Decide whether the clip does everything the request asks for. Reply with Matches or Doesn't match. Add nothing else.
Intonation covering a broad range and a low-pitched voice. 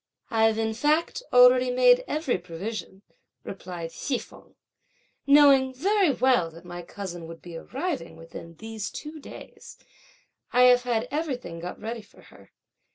Doesn't match